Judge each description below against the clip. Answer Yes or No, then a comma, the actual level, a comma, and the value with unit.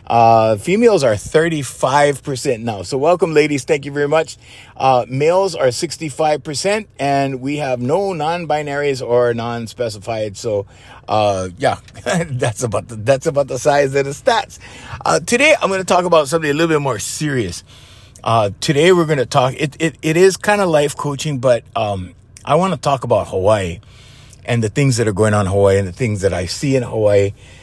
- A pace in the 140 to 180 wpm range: No, average, 190 wpm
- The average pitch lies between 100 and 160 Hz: Yes, low, 135 Hz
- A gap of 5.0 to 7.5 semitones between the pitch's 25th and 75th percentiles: Yes, wide, 5.6 semitones